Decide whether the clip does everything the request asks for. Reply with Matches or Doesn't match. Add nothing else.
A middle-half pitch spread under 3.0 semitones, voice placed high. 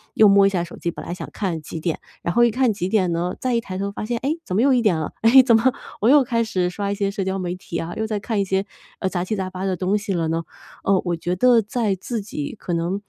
Doesn't match